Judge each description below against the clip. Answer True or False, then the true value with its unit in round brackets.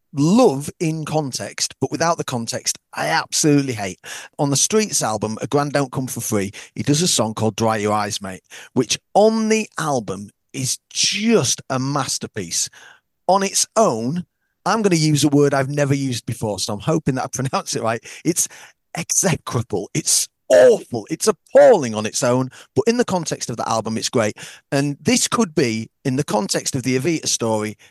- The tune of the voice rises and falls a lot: True (6.4 semitones)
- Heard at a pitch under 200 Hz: True (140 Hz)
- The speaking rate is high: False (185 wpm)